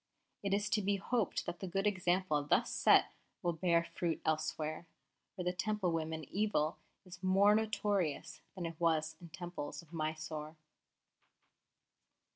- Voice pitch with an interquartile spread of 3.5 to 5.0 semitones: Yes, average, 3.8 semitones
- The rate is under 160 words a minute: Yes, average, 145 wpm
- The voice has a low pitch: No, medium, 175 Hz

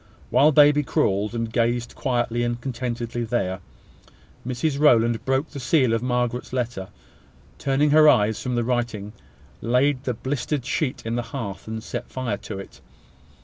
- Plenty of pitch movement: No, narrow, 2.6 semitones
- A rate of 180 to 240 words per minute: No, average, 155 wpm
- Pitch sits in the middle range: No, low, 120 Hz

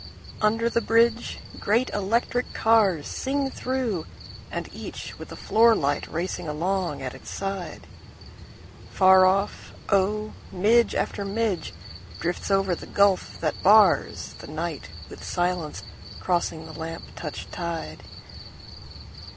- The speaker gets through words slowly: Yes, slow, 110 wpm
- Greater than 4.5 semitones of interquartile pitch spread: Yes, average, 4.9 semitones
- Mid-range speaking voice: No, high, 195 Hz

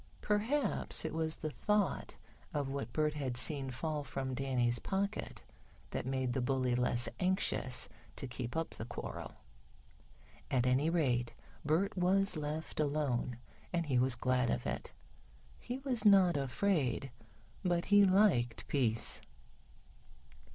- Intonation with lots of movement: Yes, wide, 6.1 semitones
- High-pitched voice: No, medium, 145 Hz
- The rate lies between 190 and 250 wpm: No, slow, 135 wpm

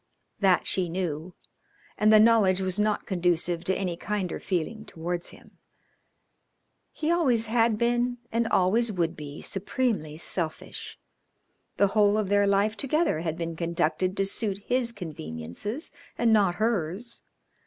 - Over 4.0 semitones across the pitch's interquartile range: Yes, average, 4.4 semitones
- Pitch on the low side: No, high, 195 Hz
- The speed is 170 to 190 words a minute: No, average, 140 wpm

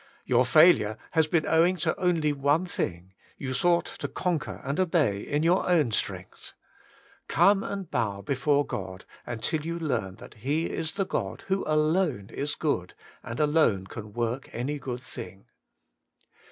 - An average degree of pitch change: No, wide, 6.0 semitones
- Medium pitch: Yes, medium, 145 Hz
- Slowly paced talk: No, average, 155 wpm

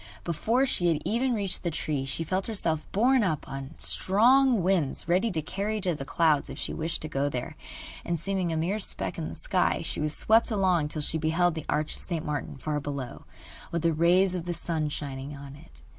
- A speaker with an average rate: No, fast, 220 wpm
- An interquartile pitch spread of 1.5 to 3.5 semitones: No, average, 4.4 semitones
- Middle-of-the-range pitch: Yes, medium, 165 Hz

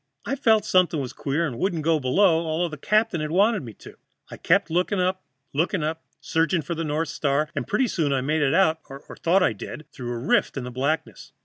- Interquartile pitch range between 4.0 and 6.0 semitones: Yes, average, 4.4 semitones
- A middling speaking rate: No, fast, 225 wpm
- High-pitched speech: No, medium, 160 Hz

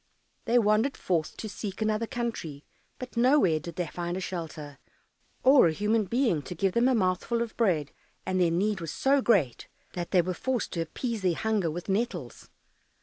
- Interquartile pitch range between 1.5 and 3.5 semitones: No, wide, 5.4 semitones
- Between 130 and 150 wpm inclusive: No, average, 190 wpm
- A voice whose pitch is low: No, high, 190 Hz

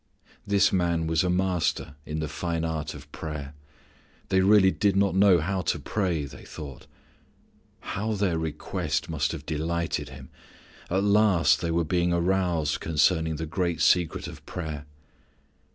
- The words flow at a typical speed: Yes, average, 155 wpm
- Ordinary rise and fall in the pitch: Yes, average, 3.4 semitones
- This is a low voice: Yes, very low, 85 Hz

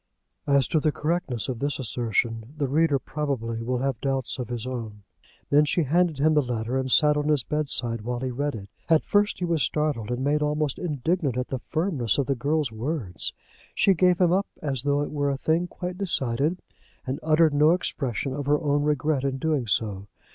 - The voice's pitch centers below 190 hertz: Yes, medium, 140 Hz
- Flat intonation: No, average, 3.7 semitones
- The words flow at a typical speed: No, fast, 210 wpm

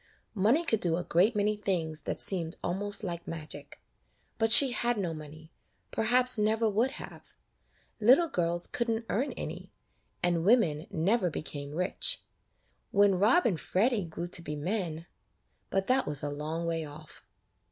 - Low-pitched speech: No, medium, 185 Hz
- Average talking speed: Yes, average, 165 wpm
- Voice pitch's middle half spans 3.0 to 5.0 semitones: No, wide, 5.5 semitones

